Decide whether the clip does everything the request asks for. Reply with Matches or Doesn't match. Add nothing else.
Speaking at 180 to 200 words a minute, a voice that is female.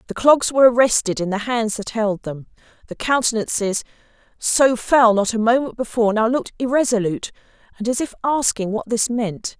Doesn't match